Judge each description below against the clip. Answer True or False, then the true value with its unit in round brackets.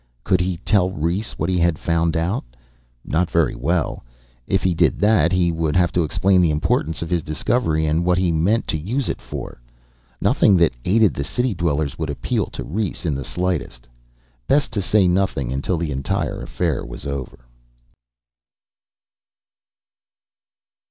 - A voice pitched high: False (85 Hz)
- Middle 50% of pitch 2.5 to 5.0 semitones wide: True (3.2 semitones)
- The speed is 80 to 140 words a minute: False (165 wpm)